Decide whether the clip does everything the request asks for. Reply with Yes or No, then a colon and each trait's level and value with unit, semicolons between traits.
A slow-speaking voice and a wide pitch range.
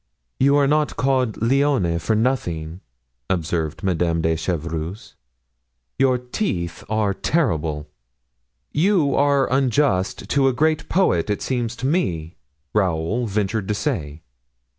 Yes: slow, 120 wpm; wide, 8.3 semitones